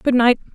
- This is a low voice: No, high, 245 Hz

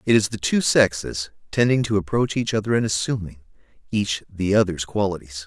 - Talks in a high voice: No, low, 100 Hz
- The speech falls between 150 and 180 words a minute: Yes, average, 175 wpm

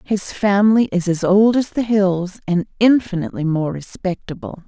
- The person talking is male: No, female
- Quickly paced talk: No, average, 155 wpm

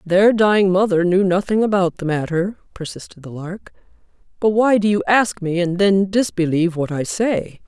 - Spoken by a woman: Yes, female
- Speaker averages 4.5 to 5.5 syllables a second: Yes, 4.9 syllables/s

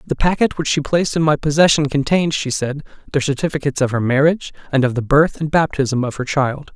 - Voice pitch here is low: No, medium, 145 Hz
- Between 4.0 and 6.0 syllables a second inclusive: No, 6.2 syllables/s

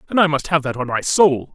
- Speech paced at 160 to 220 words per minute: No, fast, 310 wpm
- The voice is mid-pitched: Yes, medium, 150 Hz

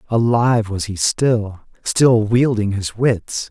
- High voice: No, low, 110 Hz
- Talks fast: No, slow, 135 wpm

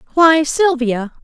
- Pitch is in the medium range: No, very high, 290 Hz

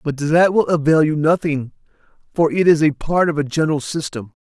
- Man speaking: Yes, male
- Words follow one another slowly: No, fast, 205 wpm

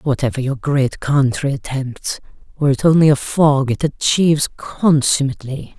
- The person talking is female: Yes, female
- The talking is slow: Yes, slow, 115 wpm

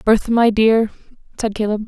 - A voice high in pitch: Yes, high, 220 Hz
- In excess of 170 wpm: No, average, 160 wpm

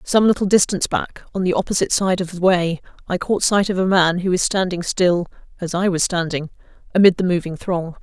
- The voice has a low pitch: No, medium, 185 Hz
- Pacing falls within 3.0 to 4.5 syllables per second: No, 5.5 syllables/s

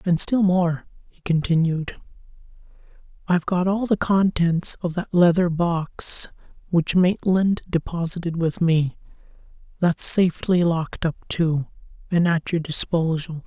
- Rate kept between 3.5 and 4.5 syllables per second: Yes, 4.2 syllables/s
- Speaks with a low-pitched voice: No, medium, 170 Hz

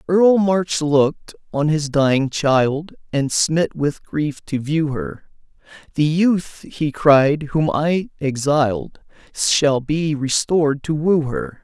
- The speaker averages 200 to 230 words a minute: No, average, 140 wpm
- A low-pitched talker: No, medium, 150 Hz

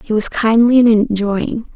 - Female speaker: Yes, female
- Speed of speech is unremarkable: Yes, average, 170 wpm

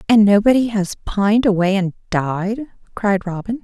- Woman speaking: Yes, female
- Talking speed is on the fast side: No, average, 150 wpm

